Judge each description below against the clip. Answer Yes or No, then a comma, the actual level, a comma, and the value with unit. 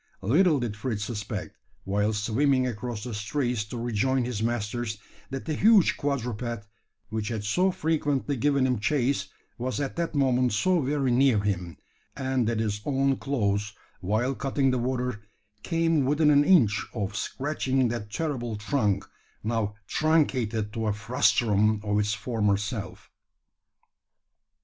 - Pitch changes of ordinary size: Yes, average, 4.6 semitones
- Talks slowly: No, average, 145 wpm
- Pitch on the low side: Yes, low, 120 Hz